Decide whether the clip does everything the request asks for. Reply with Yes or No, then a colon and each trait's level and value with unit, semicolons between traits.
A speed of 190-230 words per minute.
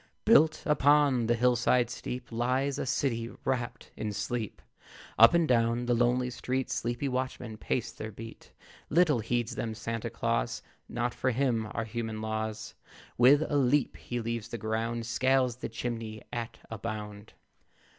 No: average, 155 wpm